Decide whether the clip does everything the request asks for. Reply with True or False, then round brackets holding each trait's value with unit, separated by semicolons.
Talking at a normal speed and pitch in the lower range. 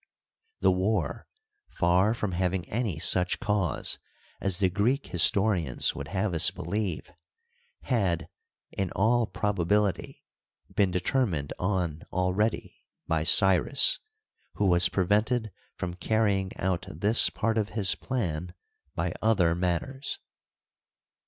False (115 wpm; 95 Hz)